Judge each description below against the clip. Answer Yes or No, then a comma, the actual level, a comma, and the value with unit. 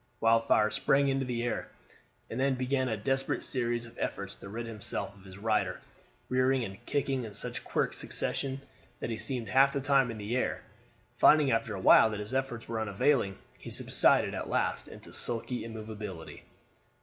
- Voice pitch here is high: No, low, 120 Hz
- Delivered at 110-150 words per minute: No, average, 175 wpm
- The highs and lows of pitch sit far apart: No, average, 3.6 semitones